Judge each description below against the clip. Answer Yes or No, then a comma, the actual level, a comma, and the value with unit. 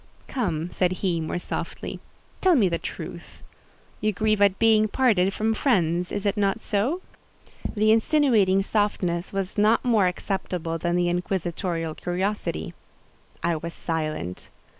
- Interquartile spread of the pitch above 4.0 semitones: No, average, 3.7 semitones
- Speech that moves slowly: Yes, slow, 130 wpm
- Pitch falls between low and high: No, high, 195 Hz